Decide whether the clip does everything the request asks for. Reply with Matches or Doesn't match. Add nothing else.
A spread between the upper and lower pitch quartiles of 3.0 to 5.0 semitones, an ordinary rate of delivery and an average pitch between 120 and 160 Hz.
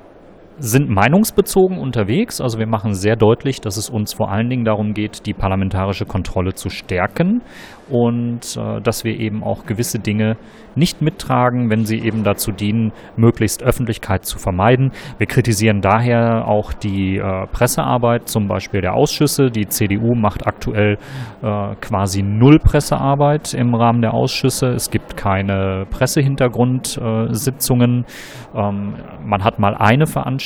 Doesn't match